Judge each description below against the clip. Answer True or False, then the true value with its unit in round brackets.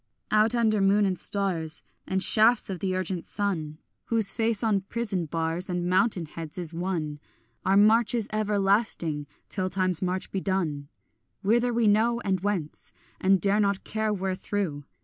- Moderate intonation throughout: True (3.2 semitones)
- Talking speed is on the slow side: False (160 wpm)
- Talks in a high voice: True (195 Hz)